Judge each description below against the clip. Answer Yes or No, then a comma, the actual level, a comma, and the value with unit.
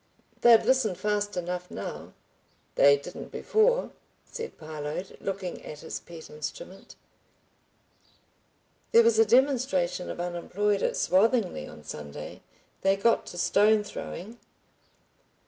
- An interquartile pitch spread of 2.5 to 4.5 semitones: No, average, 5.0 semitones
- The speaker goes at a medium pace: No, slow, 115 wpm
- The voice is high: Yes, high, 195 Hz